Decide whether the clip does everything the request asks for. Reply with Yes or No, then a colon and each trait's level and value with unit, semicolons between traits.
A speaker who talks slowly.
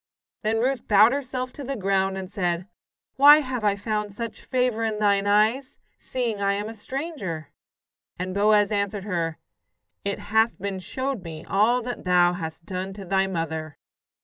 No: average, 170 wpm